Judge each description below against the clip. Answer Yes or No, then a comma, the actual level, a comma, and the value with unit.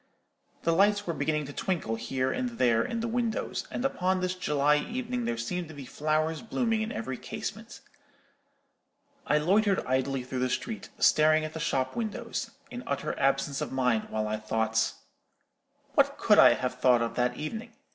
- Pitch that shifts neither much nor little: No, wide, 8.3 semitones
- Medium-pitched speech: Yes, medium, 155 Hz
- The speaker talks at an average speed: Yes, average, 175 wpm